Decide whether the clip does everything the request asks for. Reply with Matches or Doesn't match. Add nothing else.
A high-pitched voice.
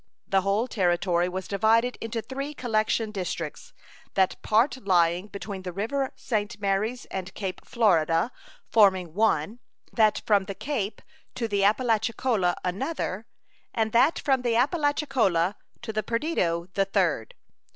Matches